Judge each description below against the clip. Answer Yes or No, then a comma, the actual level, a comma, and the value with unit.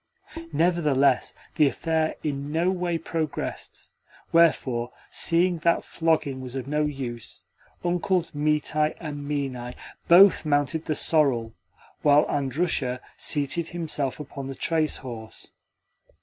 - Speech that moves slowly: Yes, slow, 115 wpm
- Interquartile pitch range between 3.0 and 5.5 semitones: Yes, average, 3.4 semitones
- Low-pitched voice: No, medium, 150 Hz